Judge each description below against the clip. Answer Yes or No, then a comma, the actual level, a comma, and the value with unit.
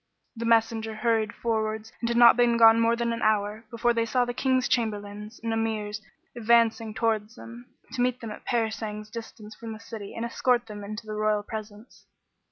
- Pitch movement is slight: Yes, narrow, 1.6 semitones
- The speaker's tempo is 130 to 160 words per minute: No, average, 195 wpm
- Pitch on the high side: Yes, high, 225 Hz